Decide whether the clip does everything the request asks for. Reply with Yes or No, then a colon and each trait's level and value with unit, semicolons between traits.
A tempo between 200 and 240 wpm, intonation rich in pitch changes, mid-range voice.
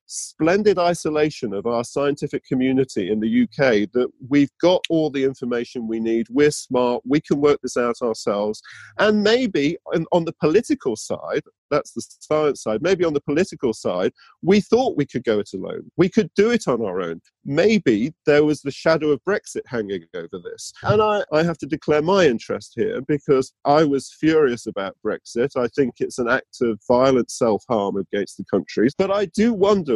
No: average, 190 wpm; wide, 7.0 semitones; medium, 150 Hz